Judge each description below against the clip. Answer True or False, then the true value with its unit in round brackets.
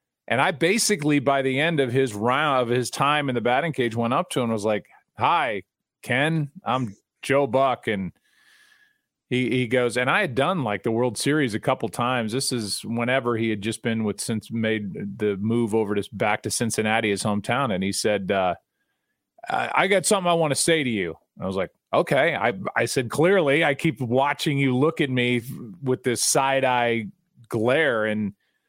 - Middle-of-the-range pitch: False (125 Hz)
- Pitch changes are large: False (4.2 semitones)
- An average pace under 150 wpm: False (200 wpm)